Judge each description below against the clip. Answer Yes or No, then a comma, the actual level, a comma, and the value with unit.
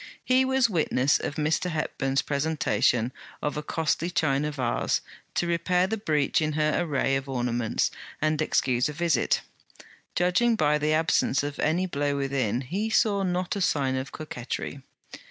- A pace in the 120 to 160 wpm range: Yes, average, 155 wpm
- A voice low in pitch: No, medium, 150 Hz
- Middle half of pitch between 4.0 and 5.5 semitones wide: Yes, average, 4.3 semitones